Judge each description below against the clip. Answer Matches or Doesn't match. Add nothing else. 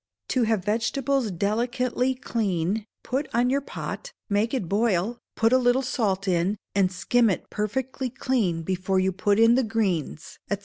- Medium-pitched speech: Doesn't match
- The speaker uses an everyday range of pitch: Matches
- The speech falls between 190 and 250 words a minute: Doesn't match